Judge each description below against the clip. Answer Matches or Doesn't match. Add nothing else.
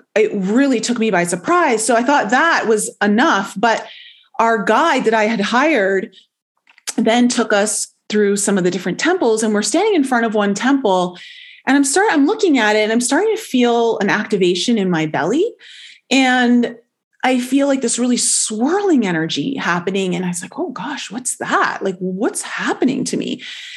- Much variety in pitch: Matches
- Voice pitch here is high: Matches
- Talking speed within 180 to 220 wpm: Matches